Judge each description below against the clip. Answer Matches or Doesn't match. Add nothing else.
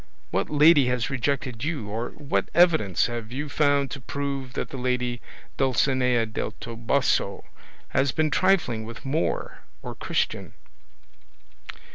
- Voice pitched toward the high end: Doesn't match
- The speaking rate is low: Matches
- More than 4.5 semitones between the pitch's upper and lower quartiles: Doesn't match